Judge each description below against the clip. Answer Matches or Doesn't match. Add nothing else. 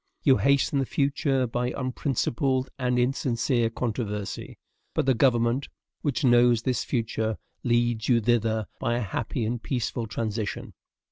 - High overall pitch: Doesn't match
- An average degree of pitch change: Doesn't match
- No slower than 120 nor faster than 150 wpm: Matches